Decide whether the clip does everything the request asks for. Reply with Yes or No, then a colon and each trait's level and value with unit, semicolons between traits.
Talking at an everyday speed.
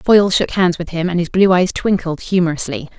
No: fast, 220 wpm